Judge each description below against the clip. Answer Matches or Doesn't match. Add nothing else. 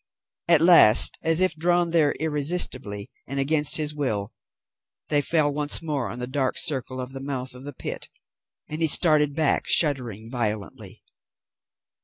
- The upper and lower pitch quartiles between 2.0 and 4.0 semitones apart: Matches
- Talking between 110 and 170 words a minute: Matches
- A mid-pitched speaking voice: Matches